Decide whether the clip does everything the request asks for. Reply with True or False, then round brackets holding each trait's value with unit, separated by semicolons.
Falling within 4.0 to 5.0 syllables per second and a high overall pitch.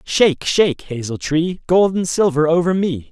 False (4.8 syllables/s; 165 Hz)